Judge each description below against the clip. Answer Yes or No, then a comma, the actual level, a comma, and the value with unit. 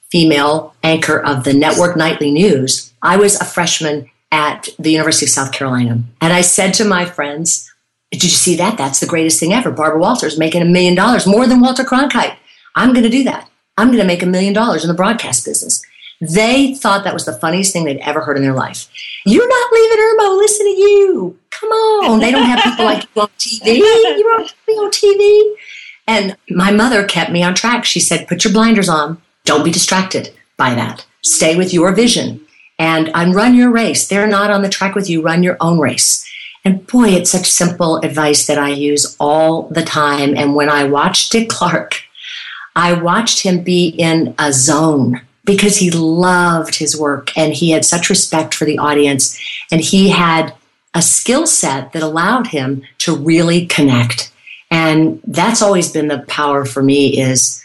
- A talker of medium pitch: Yes, medium, 175 Hz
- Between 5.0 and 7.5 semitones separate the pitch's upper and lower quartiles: Yes, average, 5.3 semitones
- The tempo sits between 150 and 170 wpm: No, average, 195 wpm